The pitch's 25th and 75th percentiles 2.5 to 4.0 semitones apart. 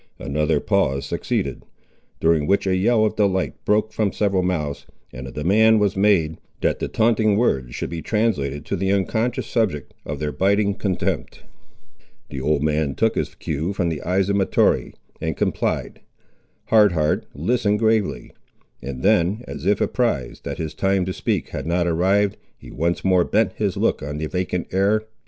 No: average, 5.2 semitones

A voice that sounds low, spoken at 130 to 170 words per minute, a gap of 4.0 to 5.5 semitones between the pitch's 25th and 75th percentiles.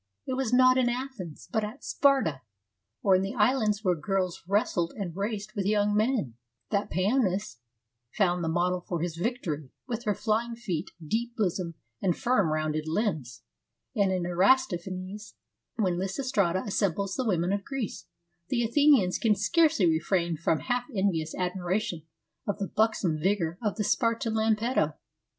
No: high, 200 Hz; average, 155 wpm; average, 4.5 semitones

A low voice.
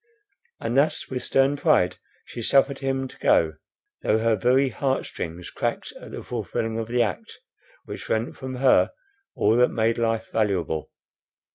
Yes: low, 115 Hz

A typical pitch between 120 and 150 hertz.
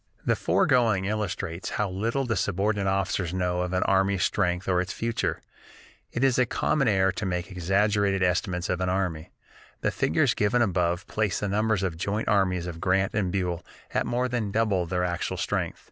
No: very low, 95 Hz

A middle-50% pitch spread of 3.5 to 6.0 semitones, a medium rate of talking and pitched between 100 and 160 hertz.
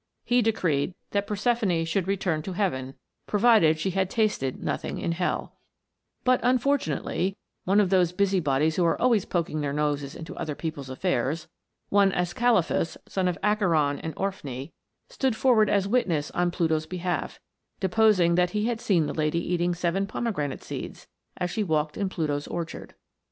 No: average, 4.5 semitones; average, 160 wpm; medium, 180 Hz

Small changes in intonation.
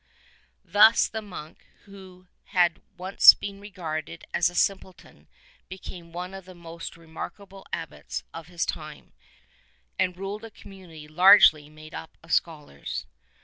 No: average, 3.0 semitones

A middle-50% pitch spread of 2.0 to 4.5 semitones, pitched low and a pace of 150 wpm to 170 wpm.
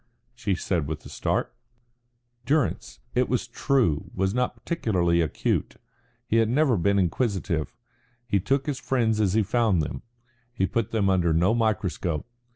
No: average, 5.2 semitones; low, 110 Hz; average, 155 wpm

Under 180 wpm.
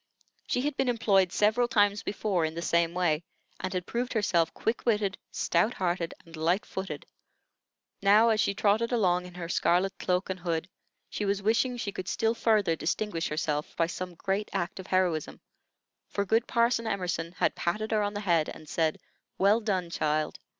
No: average, 185 wpm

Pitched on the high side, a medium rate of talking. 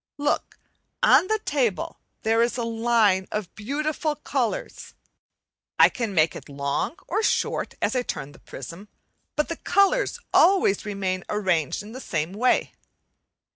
Yes: high, 225 Hz; average, 145 wpm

